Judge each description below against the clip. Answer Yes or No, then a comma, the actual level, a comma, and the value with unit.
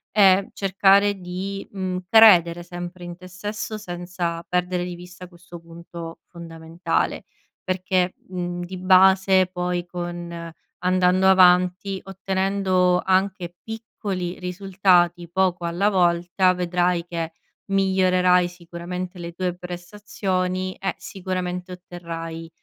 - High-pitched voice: No, medium, 180 Hz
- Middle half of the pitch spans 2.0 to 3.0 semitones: No, narrow, 1.4 semitones